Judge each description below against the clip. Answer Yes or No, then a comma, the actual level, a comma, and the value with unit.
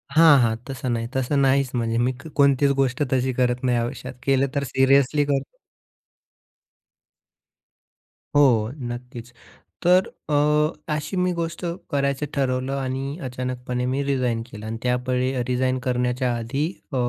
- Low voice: Yes, low, 130 Hz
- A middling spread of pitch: No, narrow, 2.1 semitones